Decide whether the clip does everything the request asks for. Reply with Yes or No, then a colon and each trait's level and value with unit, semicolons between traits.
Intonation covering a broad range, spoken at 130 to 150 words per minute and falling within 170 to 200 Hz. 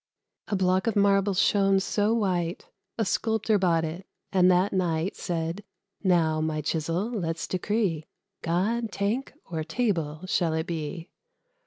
No: average, 3.7 semitones; average, 140 wpm; medium, 185 Hz